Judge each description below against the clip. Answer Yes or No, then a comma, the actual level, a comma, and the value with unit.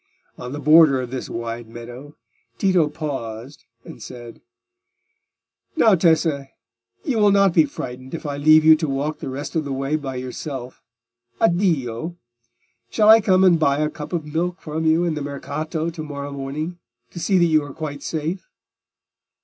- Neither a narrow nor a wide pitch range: Yes, average, 3.5 semitones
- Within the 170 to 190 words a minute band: Yes, average, 175 wpm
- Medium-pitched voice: Yes, medium, 150 Hz